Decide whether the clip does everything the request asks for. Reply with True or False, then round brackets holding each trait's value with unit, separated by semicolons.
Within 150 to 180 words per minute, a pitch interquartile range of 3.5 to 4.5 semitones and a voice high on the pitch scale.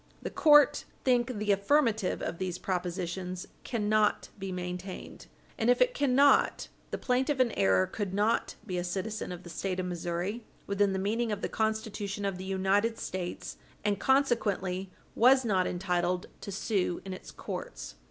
True (160 wpm; 4.0 semitones; 200 Hz)